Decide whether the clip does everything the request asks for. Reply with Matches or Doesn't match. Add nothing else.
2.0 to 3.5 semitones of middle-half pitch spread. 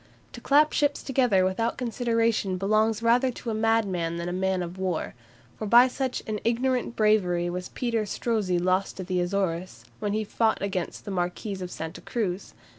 Doesn't match